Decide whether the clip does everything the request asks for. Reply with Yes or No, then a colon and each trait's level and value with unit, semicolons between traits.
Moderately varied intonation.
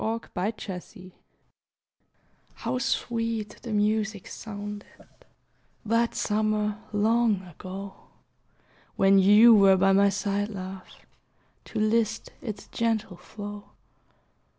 No: narrow, 2.0 semitones